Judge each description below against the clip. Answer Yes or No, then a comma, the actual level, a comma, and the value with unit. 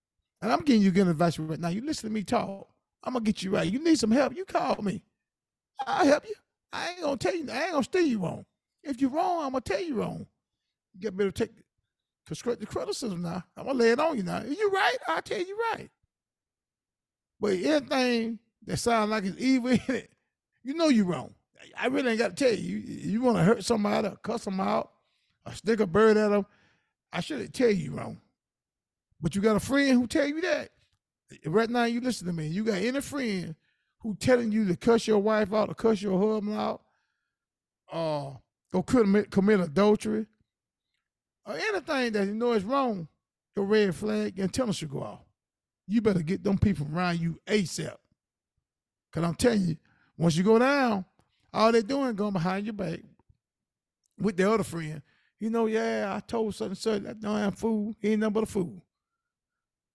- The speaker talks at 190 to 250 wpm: Yes, fast, 205 wpm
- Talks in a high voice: Yes, high, 215 Hz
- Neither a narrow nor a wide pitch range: Yes, average, 4.3 semitones